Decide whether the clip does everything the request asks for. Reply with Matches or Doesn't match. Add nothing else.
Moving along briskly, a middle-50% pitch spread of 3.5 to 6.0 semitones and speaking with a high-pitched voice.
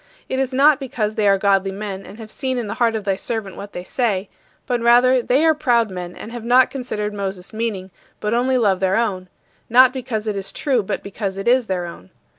Matches